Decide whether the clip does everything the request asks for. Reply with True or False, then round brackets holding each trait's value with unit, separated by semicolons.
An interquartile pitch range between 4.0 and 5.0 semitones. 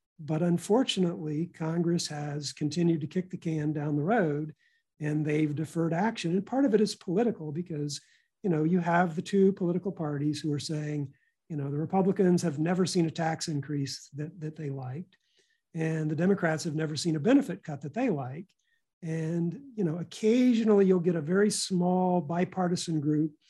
False (3.5 semitones)